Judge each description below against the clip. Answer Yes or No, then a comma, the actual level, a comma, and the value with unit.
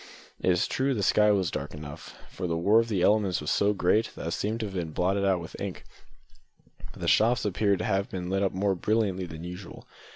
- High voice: No, very low, 95 Hz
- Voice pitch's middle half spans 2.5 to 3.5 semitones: Yes, average, 2.9 semitones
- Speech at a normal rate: No, fast, 230 wpm